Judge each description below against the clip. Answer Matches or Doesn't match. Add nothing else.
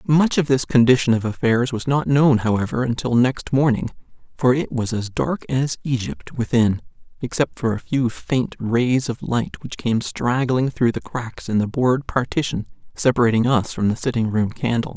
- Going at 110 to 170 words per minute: Doesn't match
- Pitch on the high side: Doesn't match